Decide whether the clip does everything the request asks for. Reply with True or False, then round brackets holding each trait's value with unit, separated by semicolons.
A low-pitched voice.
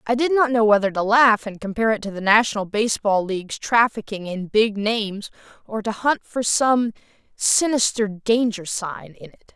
False (215 Hz)